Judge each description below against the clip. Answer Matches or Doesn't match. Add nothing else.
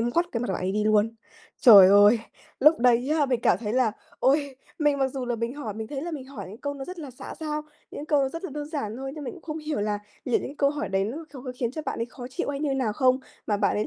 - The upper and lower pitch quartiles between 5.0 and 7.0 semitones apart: Doesn't match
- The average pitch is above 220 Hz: Matches